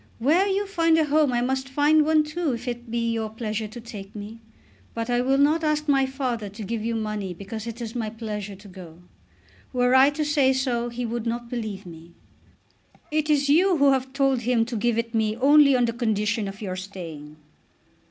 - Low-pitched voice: No, high, 240 Hz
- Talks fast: Yes, fast, 210 wpm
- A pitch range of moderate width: Yes, average, 4.4 semitones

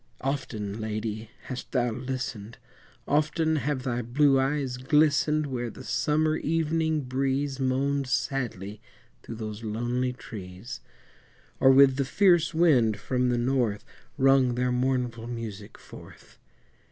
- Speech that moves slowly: Yes, slow, 125 wpm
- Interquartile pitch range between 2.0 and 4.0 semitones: Yes, average, 3.3 semitones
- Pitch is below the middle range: Yes, low, 130 Hz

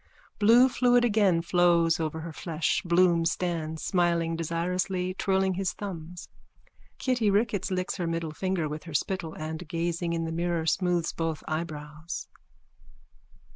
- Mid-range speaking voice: Yes, medium, 170 Hz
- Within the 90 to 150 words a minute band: Yes, slow, 135 wpm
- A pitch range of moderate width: No, narrow, 2.2 semitones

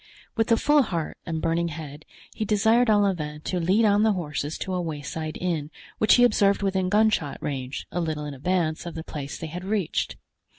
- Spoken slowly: No, average, 200 wpm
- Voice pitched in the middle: Yes, medium, 175 Hz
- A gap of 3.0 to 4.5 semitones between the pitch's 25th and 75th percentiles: No, average, 4.9 semitones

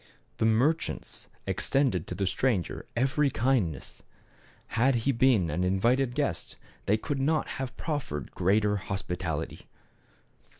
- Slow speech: Yes, slow, 125 wpm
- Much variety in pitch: Yes, wide, 6.2 semitones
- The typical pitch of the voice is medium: No, low, 115 Hz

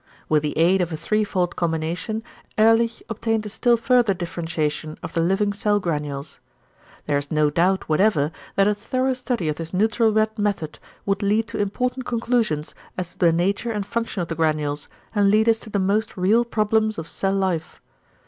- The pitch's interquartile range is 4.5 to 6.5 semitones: Yes, average, 5.1 semitones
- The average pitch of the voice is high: Yes, high, 195 Hz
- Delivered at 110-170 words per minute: No, average, 185 wpm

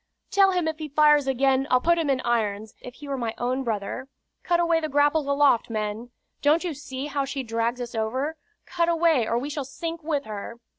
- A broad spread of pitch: No, average, 4.6 semitones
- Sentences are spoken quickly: Yes, fast, 215 wpm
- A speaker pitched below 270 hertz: No, very high, 275 Hz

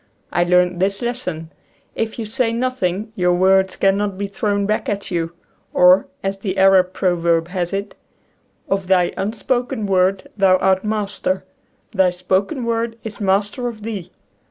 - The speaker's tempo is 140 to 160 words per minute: Yes, average, 155 wpm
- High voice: Yes, high, 195 Hz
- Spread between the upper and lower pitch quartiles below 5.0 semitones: Yes, average, 2.7 semitones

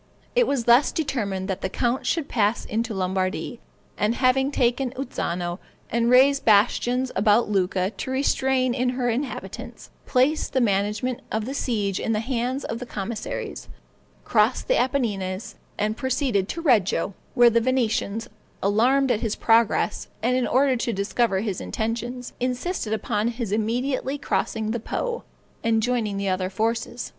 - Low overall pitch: No, high, 235 Hz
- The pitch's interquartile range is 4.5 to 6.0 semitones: No, average, 3.6 semitones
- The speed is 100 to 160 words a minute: Yes, average, 155 wpm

